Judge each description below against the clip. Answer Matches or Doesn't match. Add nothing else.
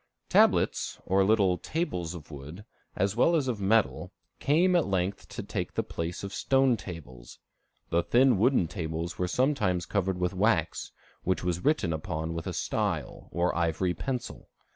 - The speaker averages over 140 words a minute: Matches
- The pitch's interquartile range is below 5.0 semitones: Doesn't match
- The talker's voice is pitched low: Matches